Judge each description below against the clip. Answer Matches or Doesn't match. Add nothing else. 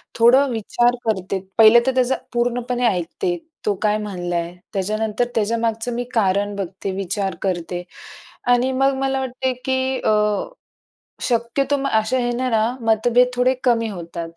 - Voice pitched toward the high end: Matches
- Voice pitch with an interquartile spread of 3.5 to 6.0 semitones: Matches